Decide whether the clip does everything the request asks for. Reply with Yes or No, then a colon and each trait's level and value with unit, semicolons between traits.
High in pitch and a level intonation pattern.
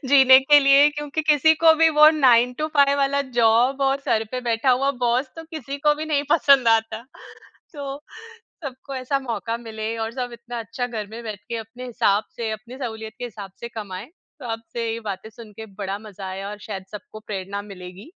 No: high, 235 Hz; average, 4.0 semitones